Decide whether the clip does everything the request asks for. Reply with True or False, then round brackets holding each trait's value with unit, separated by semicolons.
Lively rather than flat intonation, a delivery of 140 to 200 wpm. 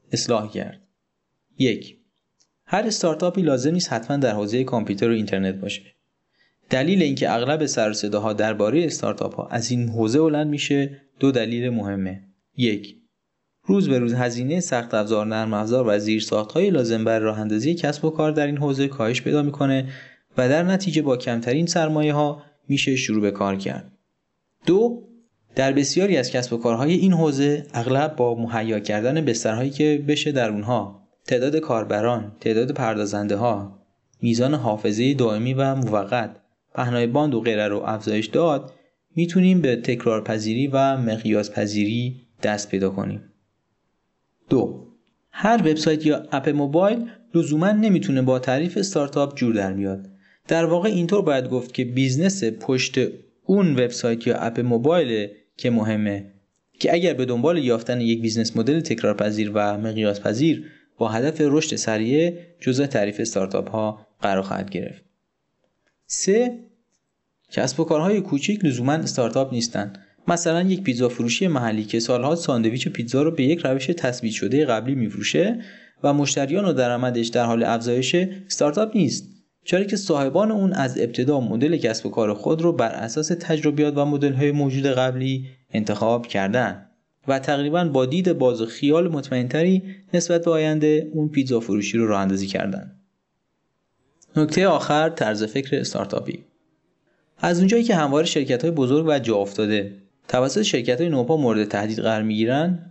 True (5.8 semitones; 150 wpm)